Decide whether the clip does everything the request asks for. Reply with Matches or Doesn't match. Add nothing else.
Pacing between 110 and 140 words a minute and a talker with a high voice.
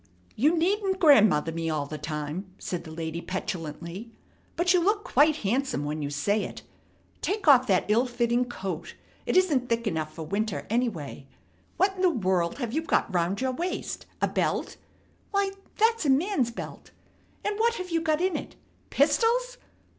Doesn't match